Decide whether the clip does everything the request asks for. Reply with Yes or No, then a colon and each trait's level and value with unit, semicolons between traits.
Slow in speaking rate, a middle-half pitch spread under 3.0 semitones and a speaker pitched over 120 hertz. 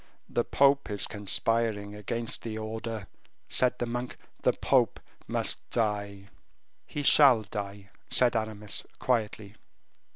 No: slow, 120 wpm; narrow, 2.6 semitones; low, 110 Hz